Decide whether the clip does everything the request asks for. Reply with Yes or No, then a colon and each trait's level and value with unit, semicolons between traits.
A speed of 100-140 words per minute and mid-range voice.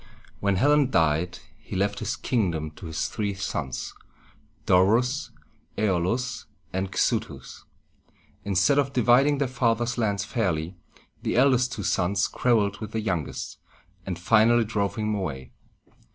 No: slow, 135 wpm; low, 105 Hz